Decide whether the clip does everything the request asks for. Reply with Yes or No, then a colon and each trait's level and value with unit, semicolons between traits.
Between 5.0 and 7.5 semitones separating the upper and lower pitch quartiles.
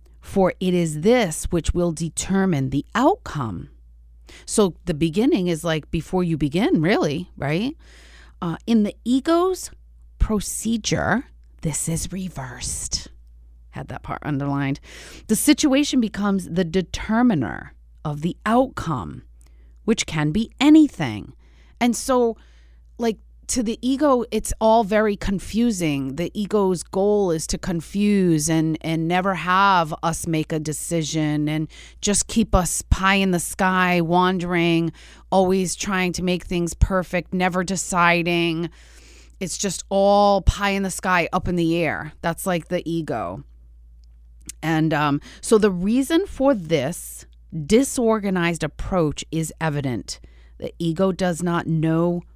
No: average, 4.6 semitones